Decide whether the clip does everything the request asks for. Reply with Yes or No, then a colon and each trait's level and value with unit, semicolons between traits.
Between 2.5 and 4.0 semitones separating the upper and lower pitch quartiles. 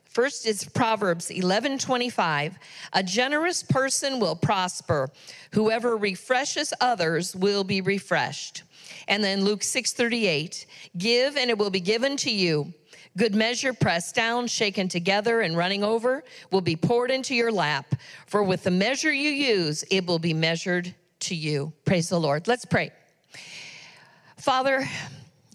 No: wide, 5.6 semitones